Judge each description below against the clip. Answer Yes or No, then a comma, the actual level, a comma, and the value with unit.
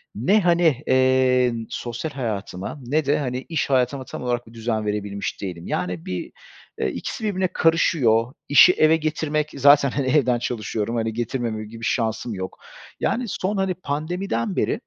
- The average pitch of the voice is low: Yes, low, 125 Hz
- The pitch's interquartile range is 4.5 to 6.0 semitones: Yes, average, 5.3 semitones